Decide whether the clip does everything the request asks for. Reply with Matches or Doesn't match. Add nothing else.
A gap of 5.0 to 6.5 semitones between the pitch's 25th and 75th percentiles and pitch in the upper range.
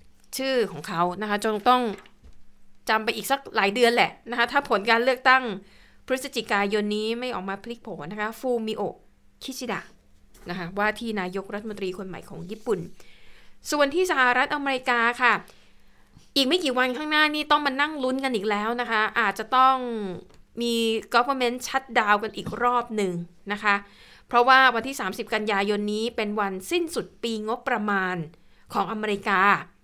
Doesn't match